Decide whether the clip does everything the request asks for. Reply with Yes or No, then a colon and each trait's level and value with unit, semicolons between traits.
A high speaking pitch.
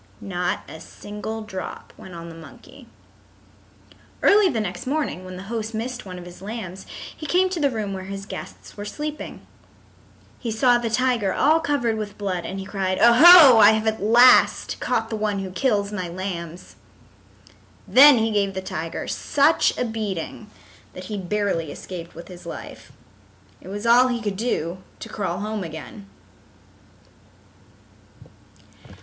Yes: high, 210 Hz